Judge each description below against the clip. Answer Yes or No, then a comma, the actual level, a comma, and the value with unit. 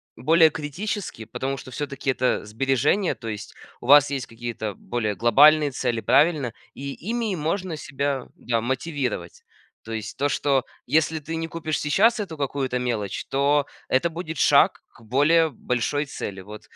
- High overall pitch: No, medium, 140 Hz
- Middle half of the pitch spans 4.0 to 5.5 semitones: Yes, average, 4.7 semitones